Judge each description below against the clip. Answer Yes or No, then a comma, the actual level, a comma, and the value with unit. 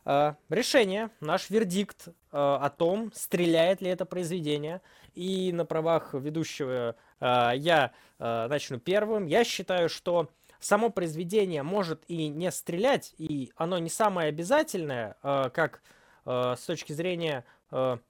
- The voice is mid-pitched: Yes, medium, 165 Hz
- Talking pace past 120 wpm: Yes, average, 135 wpm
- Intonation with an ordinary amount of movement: Yes, average, 4.5 semitones